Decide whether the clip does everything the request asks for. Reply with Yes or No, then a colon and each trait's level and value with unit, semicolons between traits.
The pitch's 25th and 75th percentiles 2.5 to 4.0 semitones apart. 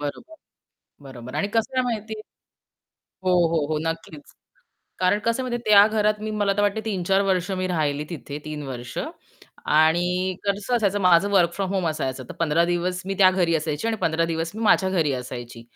No: average, 4.7 semitones